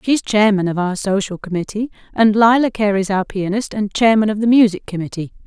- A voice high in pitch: Yes, high, 205 Hz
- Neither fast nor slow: Yes, average, 185 wpm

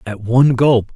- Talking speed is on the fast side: No, average, 190 wpm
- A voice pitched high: No, low, 120 Hz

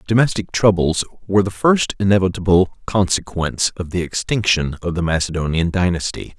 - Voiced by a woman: No, male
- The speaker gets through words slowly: Yes, slow, 130 wpm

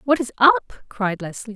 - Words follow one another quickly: No, average, 195 wpm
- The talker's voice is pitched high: Yes, high, 220 Hz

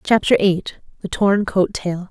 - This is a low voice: No, high, 190 Hz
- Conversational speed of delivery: Yes, average, 145 wpm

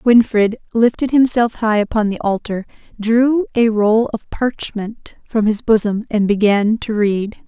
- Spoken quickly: No, average, 150 wpm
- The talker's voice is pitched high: Yes, high, 220 Hz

